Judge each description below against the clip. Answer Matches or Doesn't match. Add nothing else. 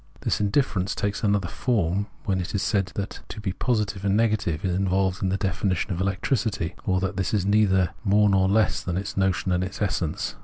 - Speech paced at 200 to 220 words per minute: Matches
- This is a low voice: Matches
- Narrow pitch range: Matches